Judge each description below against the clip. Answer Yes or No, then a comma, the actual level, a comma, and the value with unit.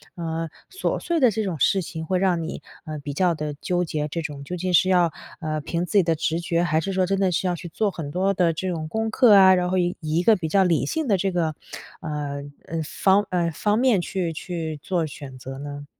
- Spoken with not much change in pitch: No, average, 3.3 semitones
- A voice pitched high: No, medium, 175 Hz